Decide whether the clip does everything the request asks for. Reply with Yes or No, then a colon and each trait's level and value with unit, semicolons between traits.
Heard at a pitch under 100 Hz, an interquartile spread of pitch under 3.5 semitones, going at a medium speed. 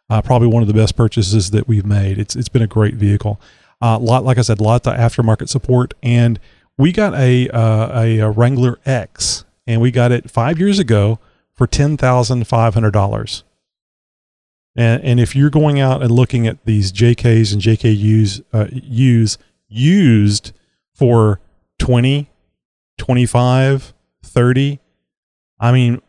No: low, 115 Hz; average, 2.8 semitones; average, 150 wpm